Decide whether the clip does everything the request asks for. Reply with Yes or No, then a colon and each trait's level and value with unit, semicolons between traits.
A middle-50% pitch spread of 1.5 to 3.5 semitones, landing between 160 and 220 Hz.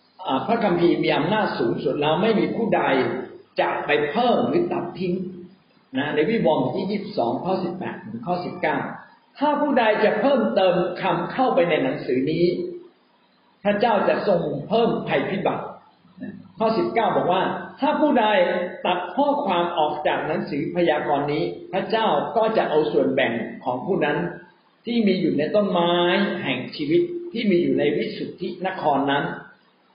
No: average, 4.6 semitones; medium, 185 Hz